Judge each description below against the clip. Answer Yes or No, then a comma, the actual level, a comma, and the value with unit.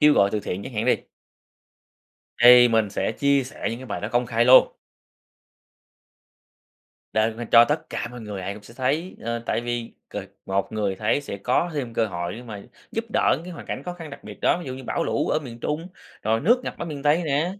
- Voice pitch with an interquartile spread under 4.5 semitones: No, average, 5.1 semitones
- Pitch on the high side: No, low, 120 Hz